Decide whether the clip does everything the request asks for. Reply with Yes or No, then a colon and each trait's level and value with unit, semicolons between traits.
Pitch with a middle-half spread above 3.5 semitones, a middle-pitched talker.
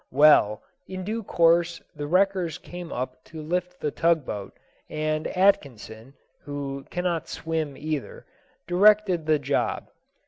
Yes: average, 3.9 semitones; medium, 160 Hz